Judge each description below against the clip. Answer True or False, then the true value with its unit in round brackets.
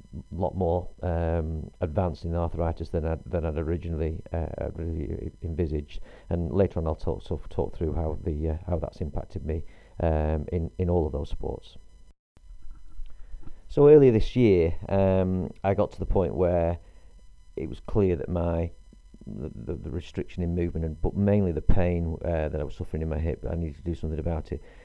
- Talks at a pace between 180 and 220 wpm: True (195 wpm)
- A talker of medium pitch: False (85 Hz)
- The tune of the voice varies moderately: False (2.2 semitones)